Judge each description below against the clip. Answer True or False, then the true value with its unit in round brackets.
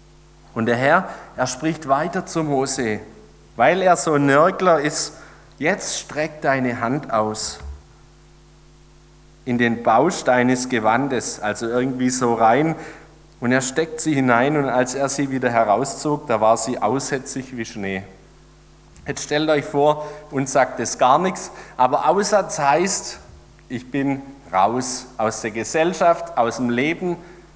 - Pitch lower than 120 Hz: False (140 Hz)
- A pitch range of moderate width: True (4.5 semitones)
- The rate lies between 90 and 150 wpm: True (145 wpm)